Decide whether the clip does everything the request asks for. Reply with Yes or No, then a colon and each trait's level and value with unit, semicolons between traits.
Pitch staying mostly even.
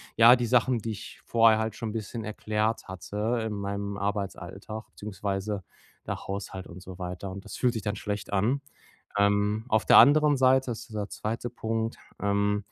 Yes: narrow, 2.1 semitones